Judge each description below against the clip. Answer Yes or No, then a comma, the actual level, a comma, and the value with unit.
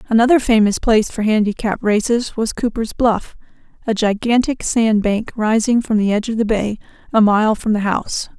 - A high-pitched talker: Yes, high, 220 Hz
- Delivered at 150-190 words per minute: Yes, average, 180 wpm